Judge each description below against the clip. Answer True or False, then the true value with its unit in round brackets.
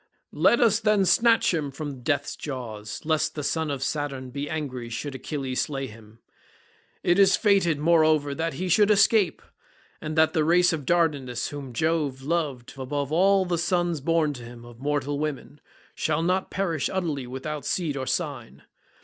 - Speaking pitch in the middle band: True (150 Hz)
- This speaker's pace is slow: False (170 wpm)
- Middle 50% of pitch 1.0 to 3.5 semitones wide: False (4.2 semitones)